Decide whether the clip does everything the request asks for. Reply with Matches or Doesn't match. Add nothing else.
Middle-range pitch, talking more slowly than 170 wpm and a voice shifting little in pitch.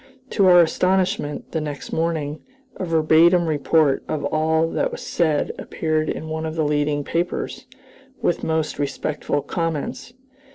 Matches